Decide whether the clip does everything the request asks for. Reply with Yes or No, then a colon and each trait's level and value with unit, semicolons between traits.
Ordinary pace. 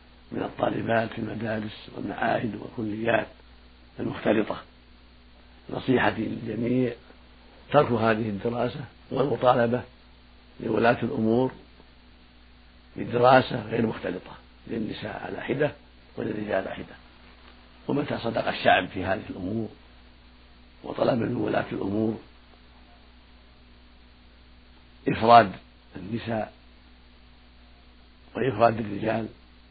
Yes: average, 75 wpm